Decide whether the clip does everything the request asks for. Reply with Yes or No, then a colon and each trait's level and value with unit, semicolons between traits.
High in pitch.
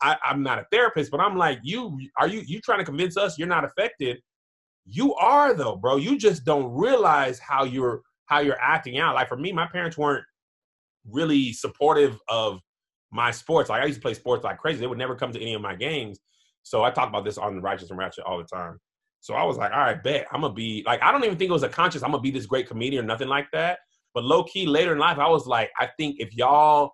No: medium, 140 Hz